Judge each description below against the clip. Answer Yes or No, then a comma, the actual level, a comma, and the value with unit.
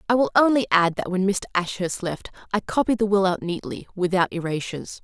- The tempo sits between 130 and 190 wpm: No, fast, 205 wpm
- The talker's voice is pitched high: Yes, high, 195 Hz